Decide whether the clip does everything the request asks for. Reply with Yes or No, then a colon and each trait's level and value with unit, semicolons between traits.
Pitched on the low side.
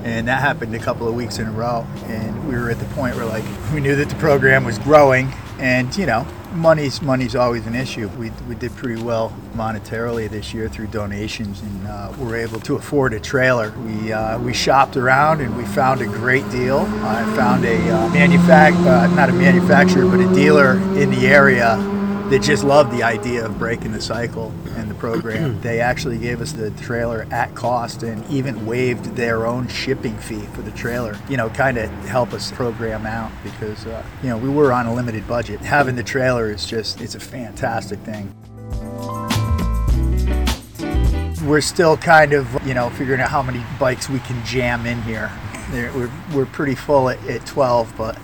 Yes: low, 120 Hz